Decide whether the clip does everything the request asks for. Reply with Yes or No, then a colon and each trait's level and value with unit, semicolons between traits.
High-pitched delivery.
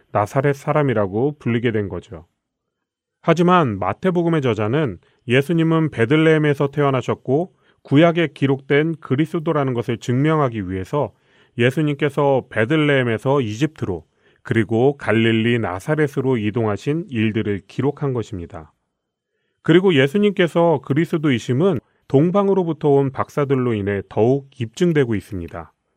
No: low, 135 Hz